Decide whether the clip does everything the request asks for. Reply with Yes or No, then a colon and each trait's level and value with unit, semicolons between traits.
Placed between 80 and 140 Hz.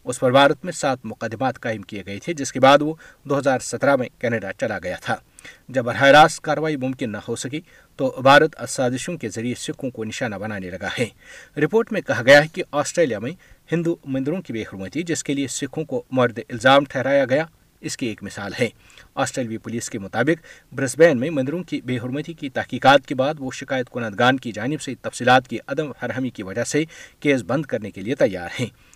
Yes: low, 135 Hz